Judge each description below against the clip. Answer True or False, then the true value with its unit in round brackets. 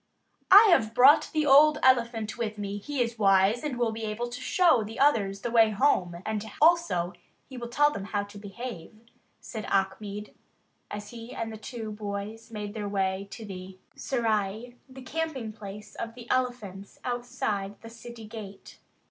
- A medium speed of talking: True (175 wpm)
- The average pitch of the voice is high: True (225 Hz)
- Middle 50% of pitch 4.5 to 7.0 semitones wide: False (3.3 semitones)